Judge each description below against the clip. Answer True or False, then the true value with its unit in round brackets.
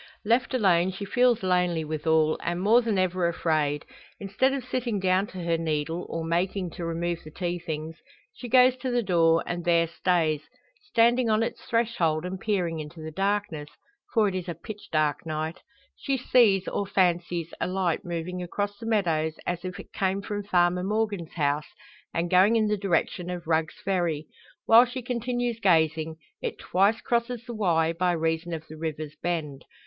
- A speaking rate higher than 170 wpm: True (180 wpm)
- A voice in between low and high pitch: True (180 Hz)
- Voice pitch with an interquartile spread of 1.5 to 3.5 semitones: False (4.3 semitones)